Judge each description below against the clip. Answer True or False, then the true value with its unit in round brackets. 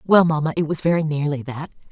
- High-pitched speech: False (155 Hz)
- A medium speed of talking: False (220 wpm)